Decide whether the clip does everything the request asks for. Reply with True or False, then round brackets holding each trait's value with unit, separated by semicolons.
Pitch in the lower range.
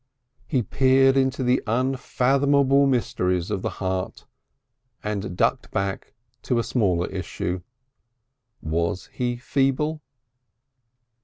True (125 Hz)